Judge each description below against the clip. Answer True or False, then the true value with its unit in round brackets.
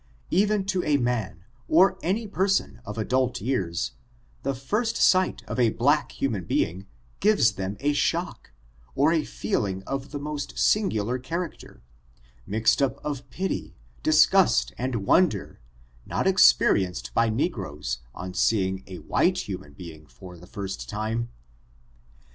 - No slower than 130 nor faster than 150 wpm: True (140 wpm)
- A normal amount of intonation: False (8.2 semitones)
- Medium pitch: False (120 Hz)